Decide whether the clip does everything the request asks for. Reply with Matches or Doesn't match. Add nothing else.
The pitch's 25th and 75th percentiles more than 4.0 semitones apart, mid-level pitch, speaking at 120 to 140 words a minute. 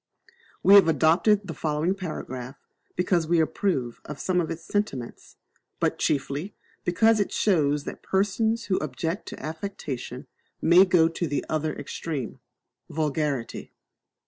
Matches